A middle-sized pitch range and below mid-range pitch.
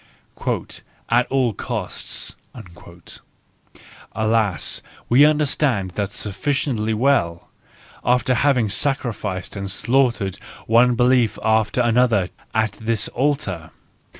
Yes: average, 3.9 semitones; low, 115 Hz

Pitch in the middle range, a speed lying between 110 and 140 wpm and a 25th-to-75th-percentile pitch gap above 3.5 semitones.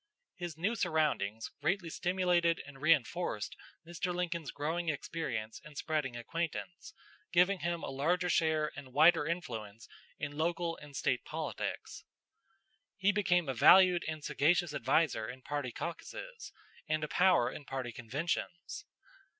Yes: medium, 160 Hz; slow, 135 wpm; average, 4.0 semitones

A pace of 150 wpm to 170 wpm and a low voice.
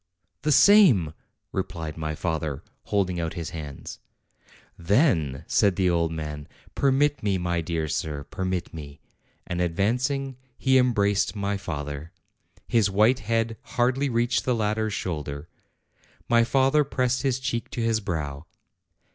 No: average, 140 wpm; low, 100 Hz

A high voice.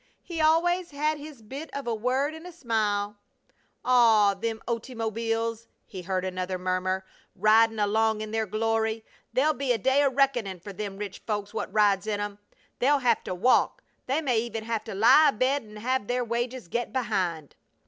Yes: high, 225 Hz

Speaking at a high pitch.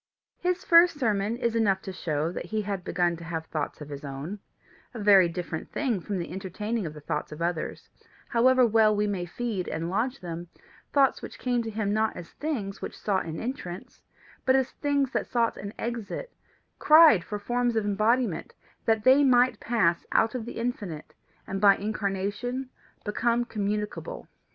Yes: high, 210 Hz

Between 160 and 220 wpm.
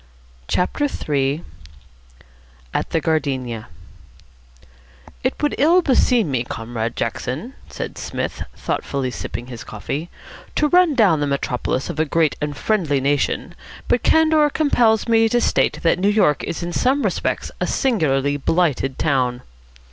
No: average, 140 wpm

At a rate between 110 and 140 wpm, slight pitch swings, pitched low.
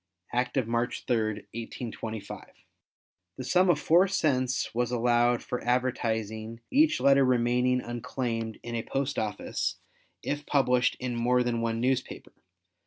Yes: slow, 135 wpm; narrow, 2.0 semitones; low, 125 Hz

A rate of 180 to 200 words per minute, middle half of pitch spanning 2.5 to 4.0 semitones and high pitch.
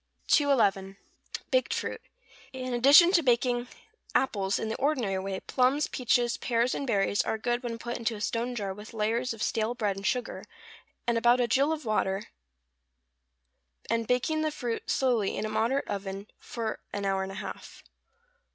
No: average, 170 wpm; average, 3.4 semitones; high, 235 Hz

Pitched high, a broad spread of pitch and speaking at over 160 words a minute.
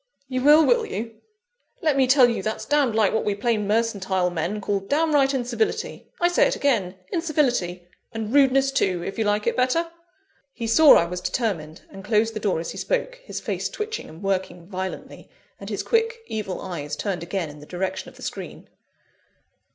Yes: high, 220 Hz; wide, 6.6 semitones; average, 190 wpm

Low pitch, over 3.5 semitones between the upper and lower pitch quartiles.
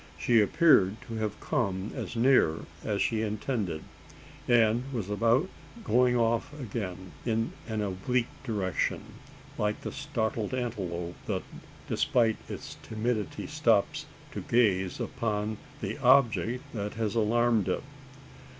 No: low, 110 Hz; average, 2.9 semitones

